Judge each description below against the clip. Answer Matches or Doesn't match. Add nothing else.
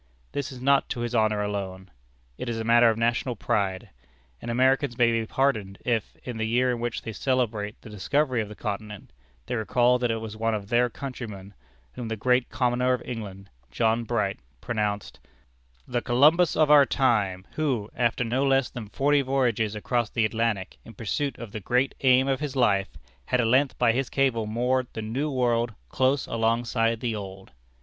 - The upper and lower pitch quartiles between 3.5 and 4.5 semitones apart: Doesn't match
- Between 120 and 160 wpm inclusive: Doesn't match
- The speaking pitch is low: Matches